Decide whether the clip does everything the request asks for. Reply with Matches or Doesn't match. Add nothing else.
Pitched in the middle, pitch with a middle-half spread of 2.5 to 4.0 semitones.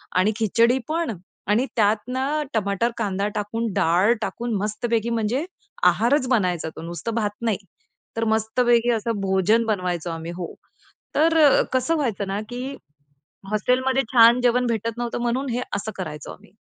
Doesn't match